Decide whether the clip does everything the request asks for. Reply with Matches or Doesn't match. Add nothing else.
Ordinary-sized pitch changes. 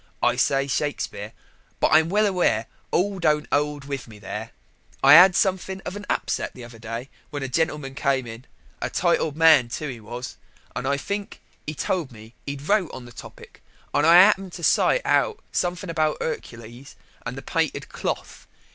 Doesn't match